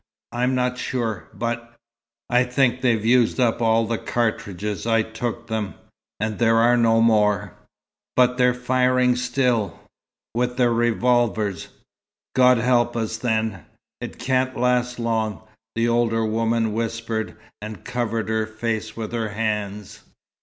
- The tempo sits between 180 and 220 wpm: No, slow, 135 wpm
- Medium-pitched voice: No, low, 115 Hz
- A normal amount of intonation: No, narrow, 2.0 semitones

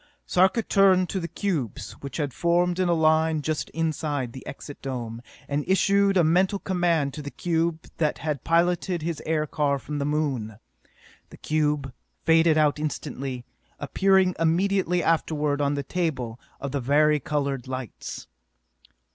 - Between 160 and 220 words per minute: No, average, 150 wpm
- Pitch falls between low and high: Yes, medium, 155 Hz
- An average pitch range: Yes, average, 3.6 semitones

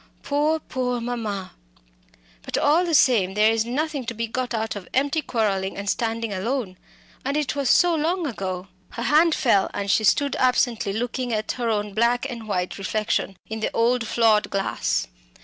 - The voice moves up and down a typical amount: Yes, average, 4.3 semitones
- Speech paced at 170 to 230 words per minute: Yes, average, 180 wpm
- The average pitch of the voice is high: Yes, high, 230 Hz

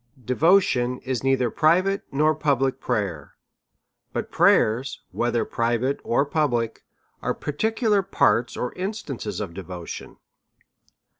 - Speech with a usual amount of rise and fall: Yes, average, 4.9 semitones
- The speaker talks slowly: Yes, slow, 105 wpm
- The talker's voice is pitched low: Yes, low, 130 Hz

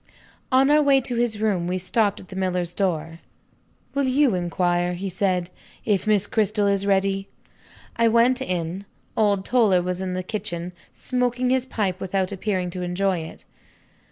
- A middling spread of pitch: Yes, average, 3.8 semitones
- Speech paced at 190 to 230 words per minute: No, average, 165 wpm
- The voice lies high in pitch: Yes, high, 195 Hz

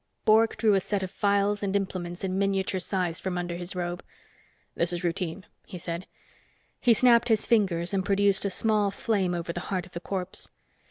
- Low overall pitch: No, high, 190 Hz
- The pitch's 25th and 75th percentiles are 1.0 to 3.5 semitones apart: Yes, narrow, 2.4 semitones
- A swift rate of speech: No, average, 195 wpm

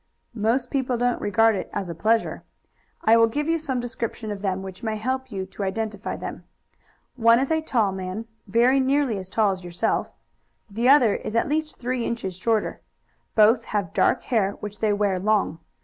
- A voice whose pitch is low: No, high, 225 Hz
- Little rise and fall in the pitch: No, average, 3.7 semitones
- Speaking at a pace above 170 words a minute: Yes, average, 190 wpm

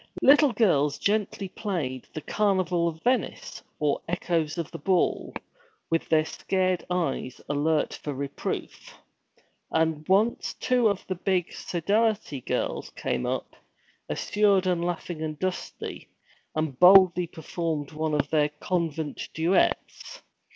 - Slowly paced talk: Yes, slow, 125 wpm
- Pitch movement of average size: Yes, average, 3.8 semitones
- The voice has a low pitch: No, medium, 170 Hz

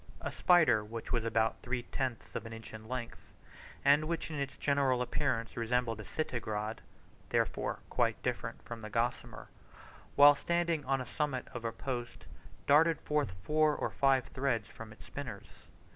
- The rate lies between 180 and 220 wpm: No, average, 165 wpm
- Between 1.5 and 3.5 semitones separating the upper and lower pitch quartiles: No, average, 4.1 semitones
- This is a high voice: No, low, 125 Hz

